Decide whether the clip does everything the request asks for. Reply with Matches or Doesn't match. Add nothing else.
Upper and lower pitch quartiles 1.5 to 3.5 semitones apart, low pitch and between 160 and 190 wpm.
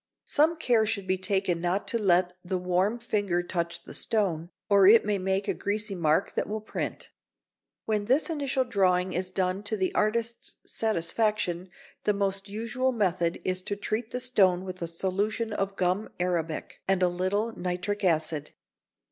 Doesn't match